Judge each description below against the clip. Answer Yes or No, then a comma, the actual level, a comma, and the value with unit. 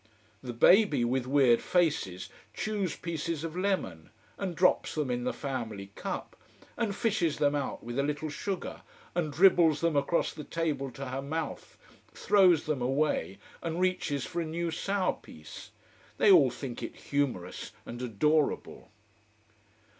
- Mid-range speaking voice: Yes, medium, 150 Hz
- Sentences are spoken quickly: No, average, 150 wpm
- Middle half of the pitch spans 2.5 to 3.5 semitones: No, average, 5.0 semitones